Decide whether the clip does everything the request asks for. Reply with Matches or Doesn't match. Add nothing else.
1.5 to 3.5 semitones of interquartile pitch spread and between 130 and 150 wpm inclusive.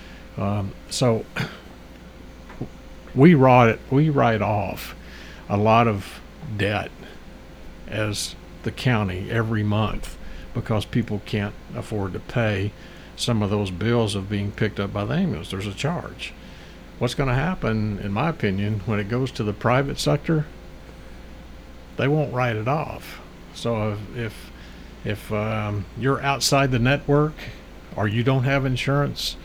Doesn't match